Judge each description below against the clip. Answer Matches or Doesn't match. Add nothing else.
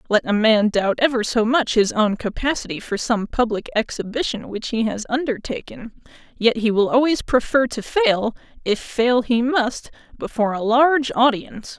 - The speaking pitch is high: Matches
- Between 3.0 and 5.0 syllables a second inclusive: Matches